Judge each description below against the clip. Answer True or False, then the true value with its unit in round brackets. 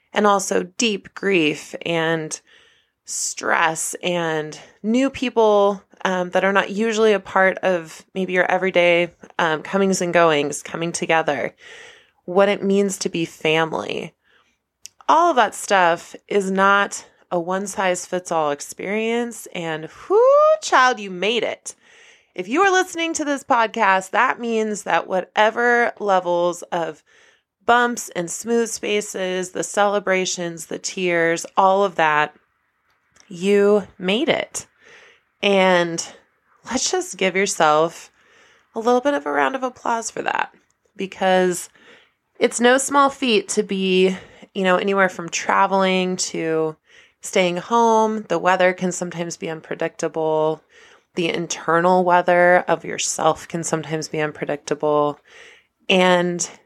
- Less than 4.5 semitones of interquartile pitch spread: False (4.8 semitones)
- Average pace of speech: False (125 wpm)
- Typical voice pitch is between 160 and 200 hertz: True (190 Hz)